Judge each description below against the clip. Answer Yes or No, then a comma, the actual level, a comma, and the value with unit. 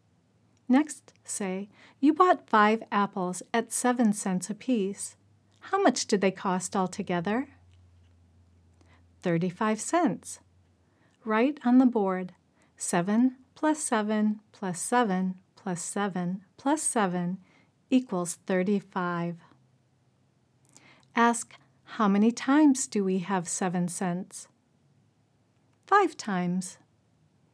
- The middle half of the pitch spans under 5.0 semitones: No, wide, 5.5 semitones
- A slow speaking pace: Yes, slow, 100 wpm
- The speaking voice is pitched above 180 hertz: Yes, high, 190 Hz